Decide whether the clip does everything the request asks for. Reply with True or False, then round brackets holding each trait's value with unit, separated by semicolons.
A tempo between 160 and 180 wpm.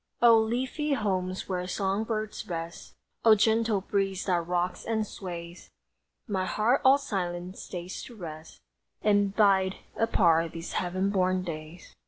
False (140 wpm)